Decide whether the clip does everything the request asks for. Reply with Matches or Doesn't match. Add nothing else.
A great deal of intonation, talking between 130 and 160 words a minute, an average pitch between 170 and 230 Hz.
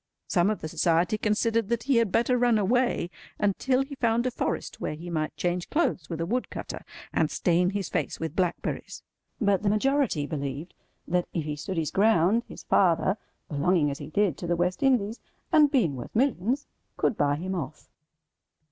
Doesn't match